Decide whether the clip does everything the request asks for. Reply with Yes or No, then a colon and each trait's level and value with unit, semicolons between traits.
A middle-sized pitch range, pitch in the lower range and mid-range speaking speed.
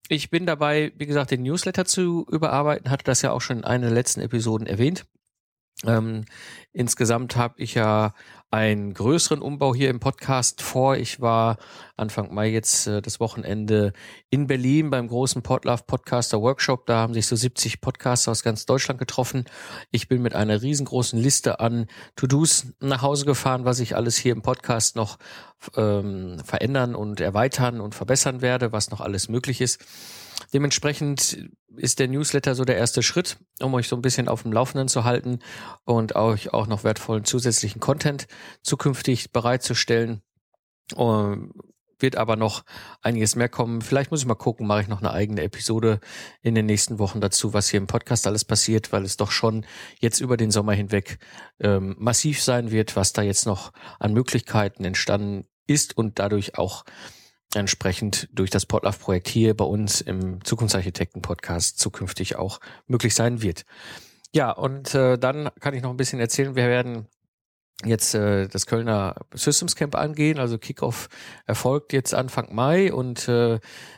Yes: average, 3.6 semitones; low, 120 Hz; average, 170 wpm